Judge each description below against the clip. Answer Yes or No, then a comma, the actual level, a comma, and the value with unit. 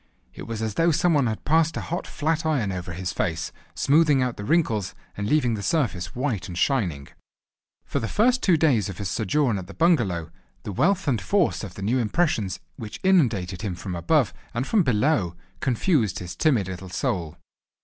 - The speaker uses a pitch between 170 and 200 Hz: No, low, 115 Hz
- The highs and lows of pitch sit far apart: Yes, wide, 8.7 semitones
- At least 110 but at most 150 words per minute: No, average, 195 wpm